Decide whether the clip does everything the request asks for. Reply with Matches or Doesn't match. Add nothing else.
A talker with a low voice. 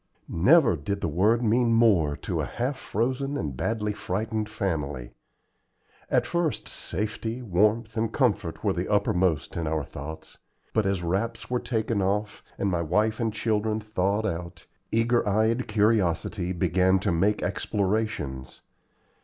Matches